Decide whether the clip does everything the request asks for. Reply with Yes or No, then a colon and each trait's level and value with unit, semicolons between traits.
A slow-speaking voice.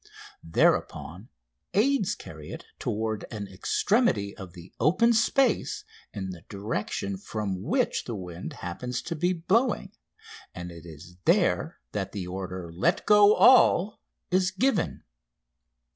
Yes: slow, 130 wpm